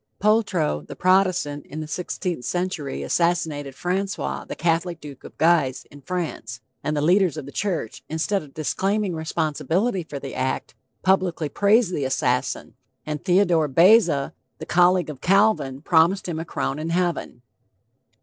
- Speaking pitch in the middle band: Yes, medium, 165 Hz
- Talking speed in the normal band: Yes, average, 150 wpm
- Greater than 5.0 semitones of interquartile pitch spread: No, average, 4.1 semitones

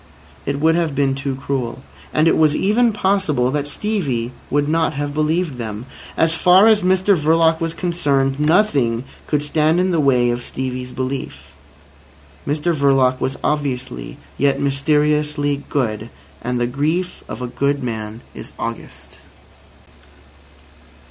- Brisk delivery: No, average, 140 wpm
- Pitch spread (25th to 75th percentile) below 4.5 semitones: Yes, average, 4.0 semitones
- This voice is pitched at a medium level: Yes, medium, 145 Hz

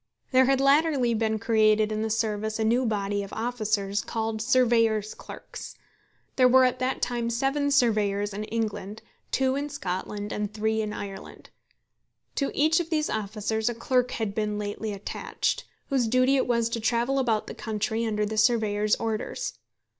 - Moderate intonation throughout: Yes, average, 3.1 semitones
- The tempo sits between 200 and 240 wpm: No, average, 170 wpm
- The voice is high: Yes, high, 225 Hz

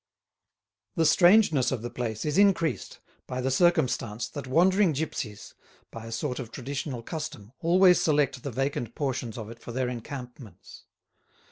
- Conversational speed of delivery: Yes, average, 150 wpm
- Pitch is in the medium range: No, low, 130 Hz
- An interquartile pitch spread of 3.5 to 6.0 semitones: Yes, average, 4.8 semitones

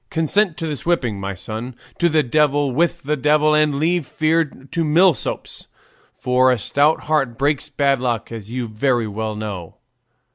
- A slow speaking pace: No, average, 170 wpm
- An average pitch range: Yes, average, 4.6 semitones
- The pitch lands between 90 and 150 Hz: Yes, medium, 140 Hz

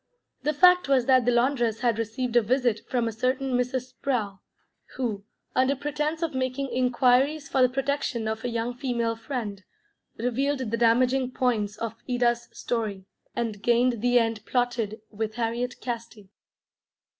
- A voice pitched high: Yes, high, 245 Hz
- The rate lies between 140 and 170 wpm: Yes, average, 155 wpm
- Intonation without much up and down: Yes, narrow, 2.2 semitones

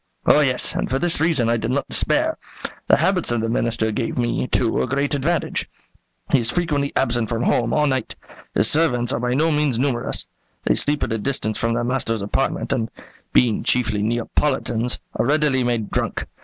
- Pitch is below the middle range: Yes, low, 125 Hz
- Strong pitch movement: No, average, 3.7 semitones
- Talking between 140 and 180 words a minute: No, average, 195 wpm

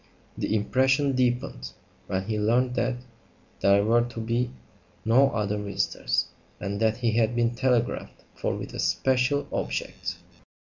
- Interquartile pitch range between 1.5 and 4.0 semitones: Yes, average, 3.2 semitones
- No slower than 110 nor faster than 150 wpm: Yes, average, 145 wpm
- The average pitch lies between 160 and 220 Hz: No, low, 115 Hz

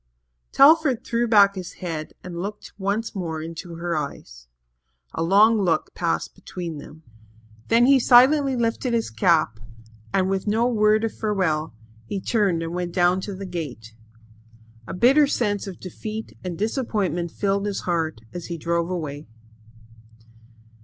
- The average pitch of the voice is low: No, high, 190 Hz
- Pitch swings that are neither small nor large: Yes, average, 4.6 semitones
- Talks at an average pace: Yes, average, 150 wpm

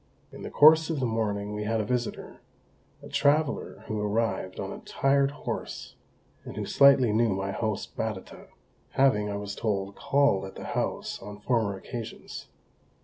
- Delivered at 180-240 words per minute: No, average, 165 wpm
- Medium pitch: No, low, 110 Hz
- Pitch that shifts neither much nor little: Yes, average, 4.7 semitones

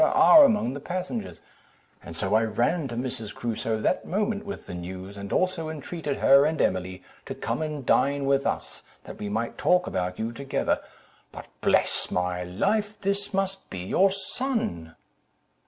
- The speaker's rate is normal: Yes, average, 165 wpm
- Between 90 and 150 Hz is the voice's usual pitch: Yes, medium, 140 Hz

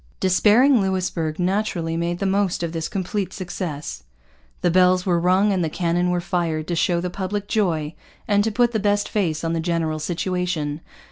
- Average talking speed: Yes, average, 185 wpm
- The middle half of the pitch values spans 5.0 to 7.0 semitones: No, average, 2.9 semitones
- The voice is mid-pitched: Yes, medium, 180 Hz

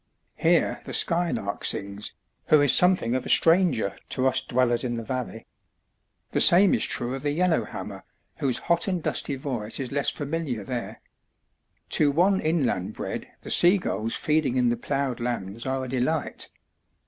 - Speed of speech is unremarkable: Yes, average, 165 wpm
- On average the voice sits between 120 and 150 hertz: Yes, low, 135 Hz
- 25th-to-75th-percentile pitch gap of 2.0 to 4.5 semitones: No, average, 5.2 semitones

